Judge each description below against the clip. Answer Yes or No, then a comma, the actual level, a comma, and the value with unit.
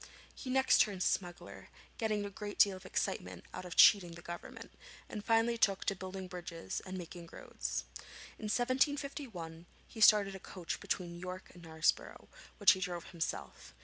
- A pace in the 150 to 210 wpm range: Yes, average, 165 wpm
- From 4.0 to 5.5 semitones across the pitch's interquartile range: No, average, 3.5 semitones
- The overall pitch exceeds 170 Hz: Yes, high, 190 Hz